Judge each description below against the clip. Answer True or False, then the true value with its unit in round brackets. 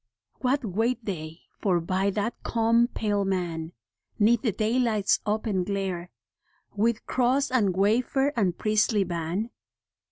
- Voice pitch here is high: True (210 Hz)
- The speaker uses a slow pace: True (125 wpm)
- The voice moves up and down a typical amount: True (3.9 semitones)